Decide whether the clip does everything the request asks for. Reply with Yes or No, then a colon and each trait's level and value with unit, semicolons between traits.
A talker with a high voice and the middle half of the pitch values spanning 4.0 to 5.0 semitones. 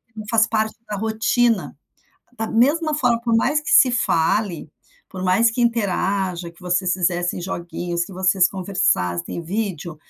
Yes: high, 195 Hz; average, 4.3 semitones